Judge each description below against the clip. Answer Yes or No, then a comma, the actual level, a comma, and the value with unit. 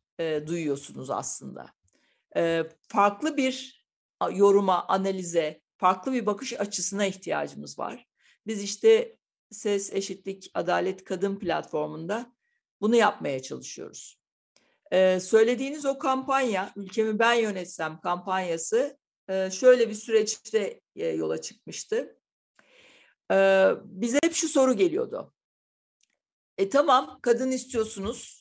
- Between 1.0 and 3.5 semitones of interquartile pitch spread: No, wide, 5.6 semitones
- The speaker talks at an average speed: No, slow, 90 wpm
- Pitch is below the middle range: No, high, 205 Hz